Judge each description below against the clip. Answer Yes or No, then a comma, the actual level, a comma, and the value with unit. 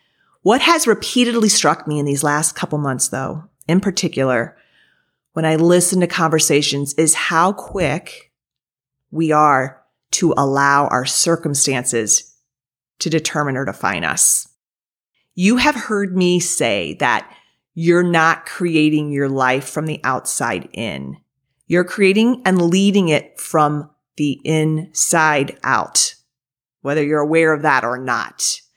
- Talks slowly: Yes, slow, 130 wpm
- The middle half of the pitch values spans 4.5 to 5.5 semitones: No, average, 4.0 semitones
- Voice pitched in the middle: Yes, medium, 155 Hz